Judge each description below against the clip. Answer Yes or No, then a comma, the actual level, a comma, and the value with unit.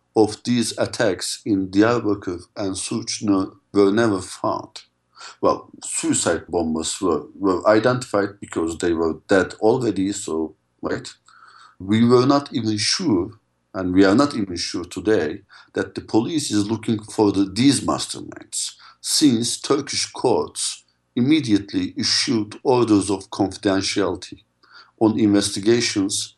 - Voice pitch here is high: No, low, 100 Hz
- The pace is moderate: No, slow, 125 wpm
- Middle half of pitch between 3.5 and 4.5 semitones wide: No, average, 2.7 semitones